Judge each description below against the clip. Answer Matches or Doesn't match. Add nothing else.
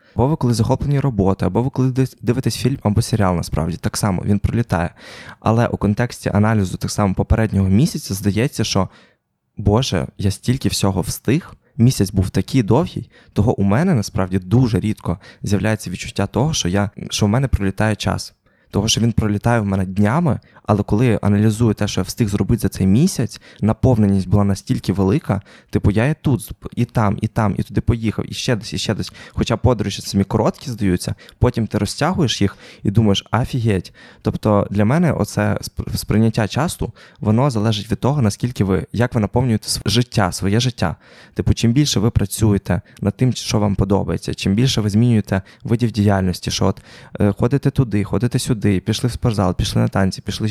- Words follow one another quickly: Matches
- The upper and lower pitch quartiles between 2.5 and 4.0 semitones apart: Matches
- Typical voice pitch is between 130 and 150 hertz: Doesn't match